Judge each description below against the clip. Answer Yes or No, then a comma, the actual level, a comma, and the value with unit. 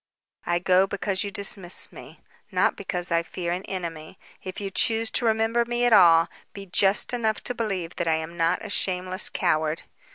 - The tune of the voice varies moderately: Yes, average, 3.7 semitones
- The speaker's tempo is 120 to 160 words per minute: No, average, 190 wpm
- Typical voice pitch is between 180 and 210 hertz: Yes, medium, 185 Hz